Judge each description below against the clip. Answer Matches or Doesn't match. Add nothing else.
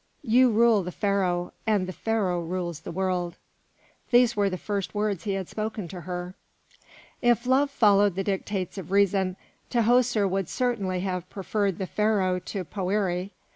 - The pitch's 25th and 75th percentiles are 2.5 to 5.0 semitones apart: Matches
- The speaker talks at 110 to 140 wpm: Doesn't match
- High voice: Matches